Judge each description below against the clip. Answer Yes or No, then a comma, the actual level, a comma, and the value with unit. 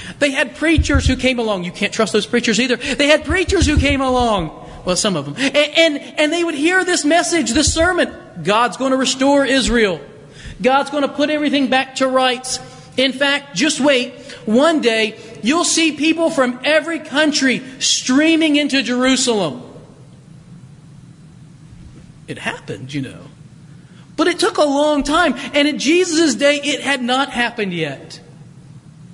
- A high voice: Yes, very high, 260 Hz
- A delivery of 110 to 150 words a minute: No, average, 165 wpm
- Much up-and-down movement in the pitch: Yes, wide, 8.6 semitones